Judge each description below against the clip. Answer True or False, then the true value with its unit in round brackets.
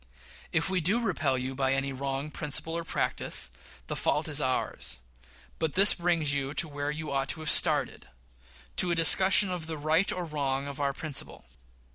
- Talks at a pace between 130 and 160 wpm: False (185 wpm)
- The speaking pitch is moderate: True (150 Hz)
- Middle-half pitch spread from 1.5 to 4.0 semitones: True (3.5 semitones)